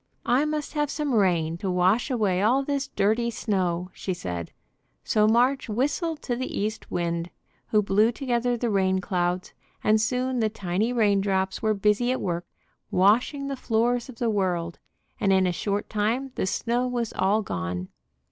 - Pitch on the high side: Yes, high, 215 Hz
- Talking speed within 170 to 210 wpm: Yes, average, 175 wpm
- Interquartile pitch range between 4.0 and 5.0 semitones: Yes, average, 4.6 semitones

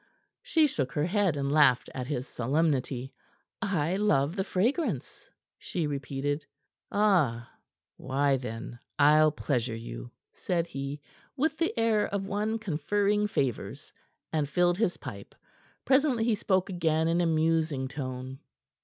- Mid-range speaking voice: Yes, medium, 155 Hz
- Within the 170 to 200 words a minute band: No, slow, 135 wpm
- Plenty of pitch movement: Yes, wide, 6.8 semitones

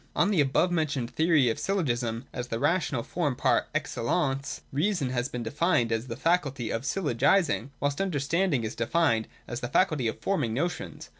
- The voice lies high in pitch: No, medium, 140 Hz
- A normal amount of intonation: No, wide, 5.9 semitones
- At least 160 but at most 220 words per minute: Yes, average, 175 wpm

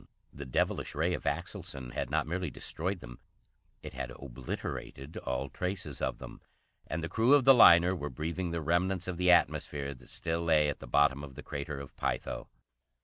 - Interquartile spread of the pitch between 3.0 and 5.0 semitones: Yes, average, 4.3 semitones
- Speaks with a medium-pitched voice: No, very low, 80 Hz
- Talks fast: No, average, 190 wpm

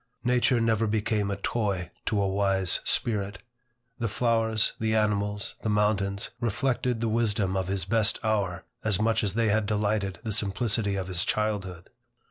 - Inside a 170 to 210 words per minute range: No, average, 160 wpm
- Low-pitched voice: Yes, low, 105 Hz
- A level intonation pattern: Yes, narrow, 2.2 semitones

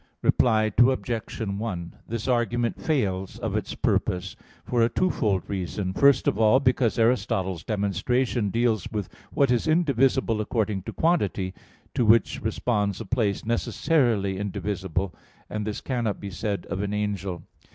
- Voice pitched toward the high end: No, low, 110 Hz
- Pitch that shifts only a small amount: No, average, 3.6 semitones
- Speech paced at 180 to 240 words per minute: No, average, 140 wpm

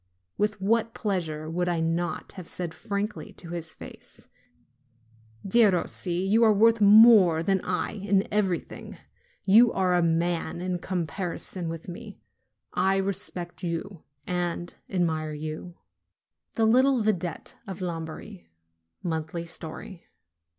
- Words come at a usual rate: No, slow, 120 wpm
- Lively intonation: No, average, 3.2 semitones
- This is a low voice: No, medium, 180 Hz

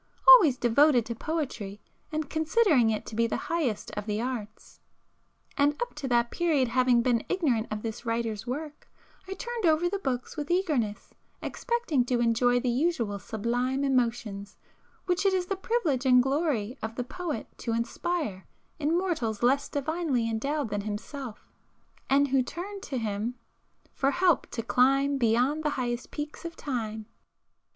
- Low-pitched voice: No, very high, 260 Hz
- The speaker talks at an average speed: Yes, average, 160 wpm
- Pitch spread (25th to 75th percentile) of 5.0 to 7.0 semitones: Yes, average, 5.3 semitones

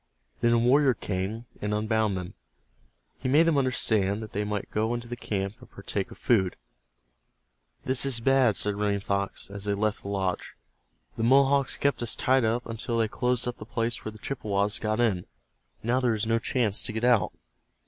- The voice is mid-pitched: No, low, 110 Hz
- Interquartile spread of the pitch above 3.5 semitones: No, average, 3.1 semitones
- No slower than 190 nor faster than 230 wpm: Yes, average, 195 wpm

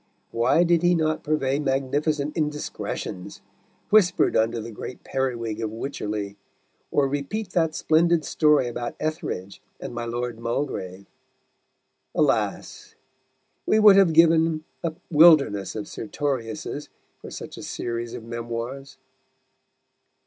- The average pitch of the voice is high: No, medium, 140 Hz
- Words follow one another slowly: Yes, slow, 120 wpm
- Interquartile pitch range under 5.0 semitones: No, average, 5.3 semitones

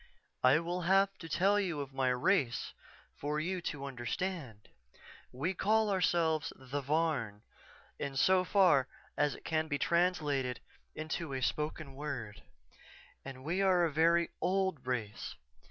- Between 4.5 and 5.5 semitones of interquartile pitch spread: Yes, average, 5.0 semitones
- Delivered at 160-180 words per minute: No, average, 140 wpm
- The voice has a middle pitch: Yes, medium, 155 Hz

